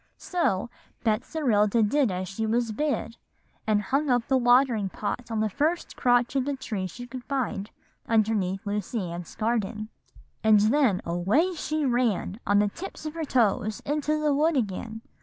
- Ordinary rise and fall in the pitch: Yes, average, 4.8 semitones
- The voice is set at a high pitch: Yes, high, 230 Hz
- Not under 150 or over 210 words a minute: Yes, average, 165 wpm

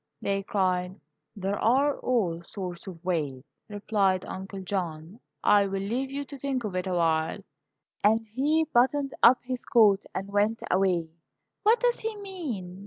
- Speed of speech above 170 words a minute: No, average, 155 wpm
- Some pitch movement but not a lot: No, wide, 5.7 semitones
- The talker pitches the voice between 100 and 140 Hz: No, high, 200 Hz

